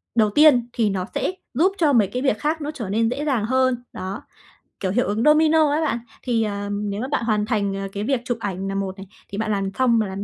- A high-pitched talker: Yes, high, 225 Hz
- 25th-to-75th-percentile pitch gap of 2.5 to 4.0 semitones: No, average, 4.8 semitones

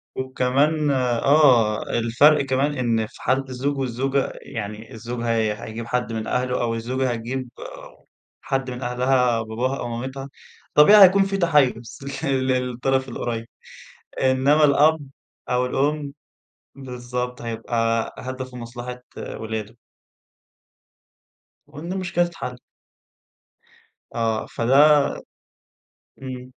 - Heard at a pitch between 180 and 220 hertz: No, low, 125 Hz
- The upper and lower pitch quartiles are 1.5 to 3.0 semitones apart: Yes, average, 2.7 semitones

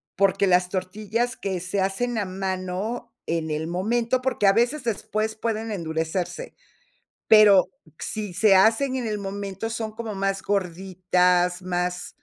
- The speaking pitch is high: Yes, high, 195 Hz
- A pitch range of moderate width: Yes, average, 3.4 semitones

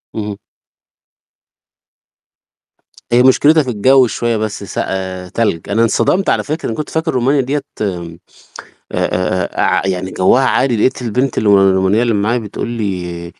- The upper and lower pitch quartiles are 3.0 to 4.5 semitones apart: No, average, 5.1 semitones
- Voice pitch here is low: Yes, low, 110 Hz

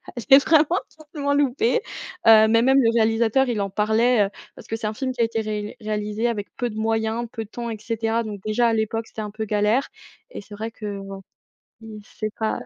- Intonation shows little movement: Yes, narrow, 1.9 semitones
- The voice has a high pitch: Yes, high, 225 Hz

